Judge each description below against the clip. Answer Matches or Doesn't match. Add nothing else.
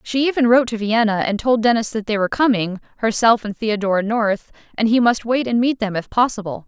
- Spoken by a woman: Matches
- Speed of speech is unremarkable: Doesn't match